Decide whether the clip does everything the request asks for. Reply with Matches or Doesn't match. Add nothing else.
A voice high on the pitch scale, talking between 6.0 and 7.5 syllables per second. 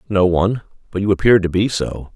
Doesn't match